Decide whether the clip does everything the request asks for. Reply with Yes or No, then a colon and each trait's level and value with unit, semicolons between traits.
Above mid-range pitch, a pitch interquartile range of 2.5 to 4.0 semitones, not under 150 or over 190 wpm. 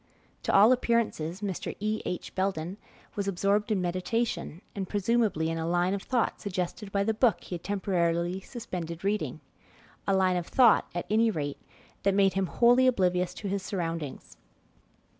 Yes: high, 195 Hz; average, 3.2 semitones; average, 165 wpm